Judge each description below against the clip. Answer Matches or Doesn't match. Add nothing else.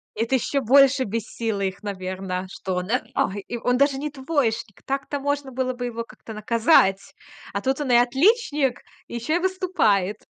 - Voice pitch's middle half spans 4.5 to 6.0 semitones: Matches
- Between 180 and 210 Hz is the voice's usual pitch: Doesn't match